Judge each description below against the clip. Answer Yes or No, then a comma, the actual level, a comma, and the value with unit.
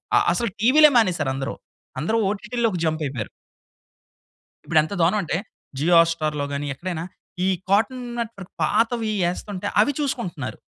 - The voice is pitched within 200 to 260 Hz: No, medium, 185 Hz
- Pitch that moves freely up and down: Yes, wide, 6.4 semitones